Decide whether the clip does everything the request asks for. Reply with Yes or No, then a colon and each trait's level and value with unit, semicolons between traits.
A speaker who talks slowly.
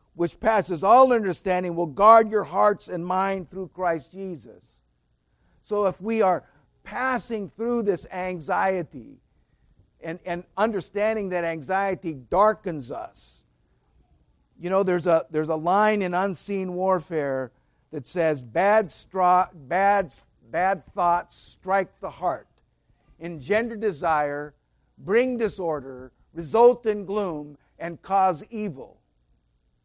Yes: slow, 115 wpm